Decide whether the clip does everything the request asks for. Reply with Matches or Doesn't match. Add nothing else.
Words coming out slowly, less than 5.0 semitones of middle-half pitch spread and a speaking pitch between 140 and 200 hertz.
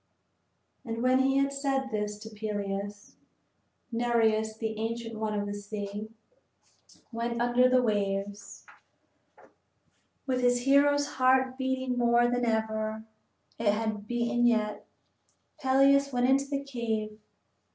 Doesn't match